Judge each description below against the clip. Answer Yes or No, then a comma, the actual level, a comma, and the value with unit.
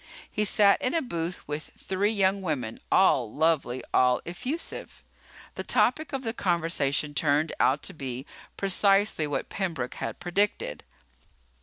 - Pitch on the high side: No, medium, 170 Hz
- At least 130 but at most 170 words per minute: Yes, average, 140 wpm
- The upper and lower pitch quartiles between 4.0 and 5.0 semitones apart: No, wide, 5.6 semitones